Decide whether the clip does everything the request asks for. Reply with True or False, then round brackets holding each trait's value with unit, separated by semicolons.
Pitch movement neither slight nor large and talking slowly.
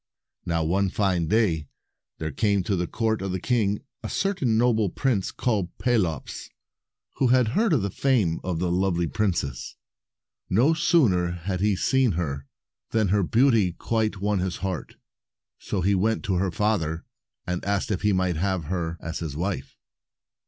False (4.1 semitones; 170 wpm)